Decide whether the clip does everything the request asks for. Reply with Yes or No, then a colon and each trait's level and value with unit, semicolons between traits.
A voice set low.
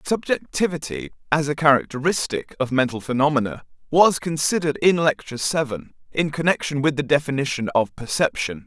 No: medium, 145 Hz